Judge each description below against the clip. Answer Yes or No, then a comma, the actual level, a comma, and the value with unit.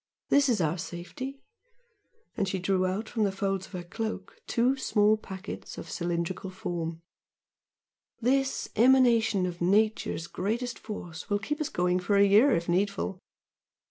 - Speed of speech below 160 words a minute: Yes, average, 150 wpm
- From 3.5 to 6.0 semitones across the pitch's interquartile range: Yes, average, 4.2 semitones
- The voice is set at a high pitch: Yes, high, 200 Hz